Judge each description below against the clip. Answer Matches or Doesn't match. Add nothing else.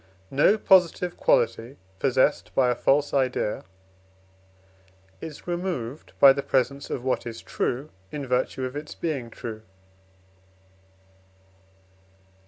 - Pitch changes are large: Doesn't match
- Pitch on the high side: Doesn't match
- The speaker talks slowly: Matches